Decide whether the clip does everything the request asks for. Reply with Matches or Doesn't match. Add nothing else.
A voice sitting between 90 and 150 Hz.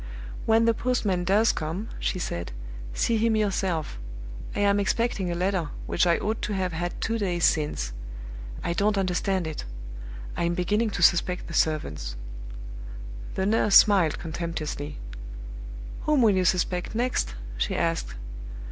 Doesn't match